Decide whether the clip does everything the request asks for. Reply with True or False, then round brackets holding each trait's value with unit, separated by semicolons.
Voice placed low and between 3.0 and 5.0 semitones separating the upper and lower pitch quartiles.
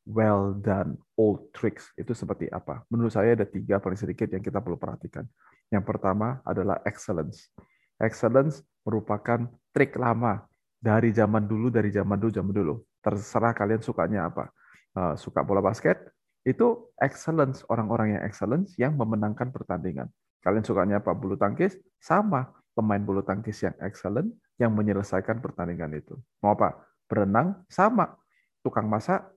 True (110 Hz; 3.4 semitones)